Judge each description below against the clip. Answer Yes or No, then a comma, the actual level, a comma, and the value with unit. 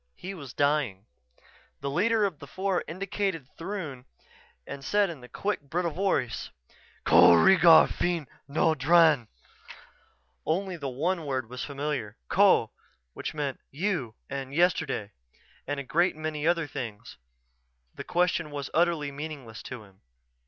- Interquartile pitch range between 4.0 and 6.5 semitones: Yes, average, 4.5 semitones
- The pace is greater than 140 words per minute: No, slow, 135 wpm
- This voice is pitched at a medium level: Yes, medium, 150 Hz